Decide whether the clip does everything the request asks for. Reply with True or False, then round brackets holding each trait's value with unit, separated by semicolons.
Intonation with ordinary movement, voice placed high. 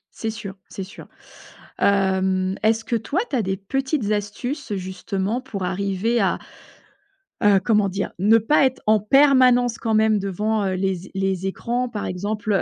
True (3.2 semitones; 210 Hz)